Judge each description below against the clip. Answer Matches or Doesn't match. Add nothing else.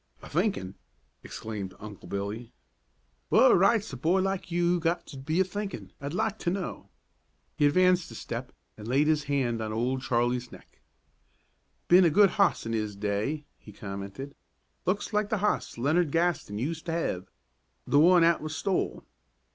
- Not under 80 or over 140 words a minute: Doesn't match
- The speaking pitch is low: Doesn't match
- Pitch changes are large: Matches